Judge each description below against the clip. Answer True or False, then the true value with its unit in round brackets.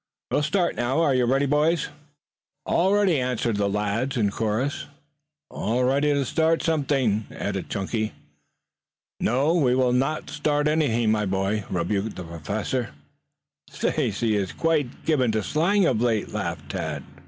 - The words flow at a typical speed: True (150 wpm)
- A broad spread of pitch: True (5.7 semitones)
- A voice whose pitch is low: True (125 Hz)